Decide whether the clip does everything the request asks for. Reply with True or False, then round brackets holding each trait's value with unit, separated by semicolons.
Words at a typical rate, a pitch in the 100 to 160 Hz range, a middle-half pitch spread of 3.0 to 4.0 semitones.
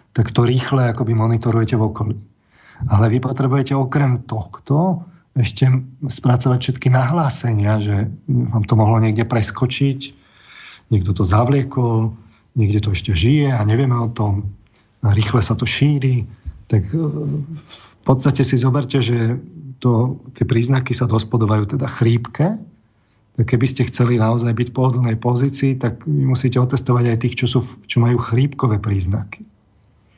True (145 wpm; 120 Hz; 3.3 semitones)